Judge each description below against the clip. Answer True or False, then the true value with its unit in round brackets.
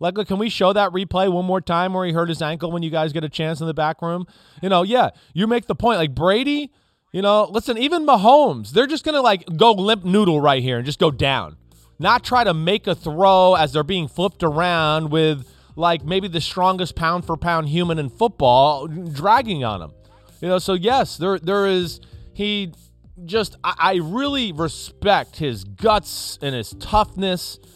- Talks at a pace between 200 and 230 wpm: True (205 wpm)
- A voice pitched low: False (175 Hz)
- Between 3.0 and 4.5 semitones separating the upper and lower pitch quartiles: True (4.1 semitones)